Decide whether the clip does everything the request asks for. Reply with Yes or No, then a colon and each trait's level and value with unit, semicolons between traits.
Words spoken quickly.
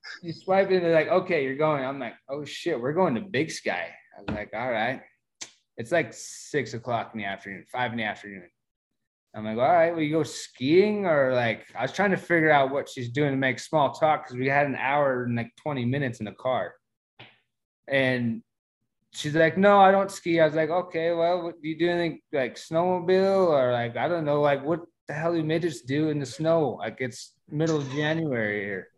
Yes: fast, 220 wpm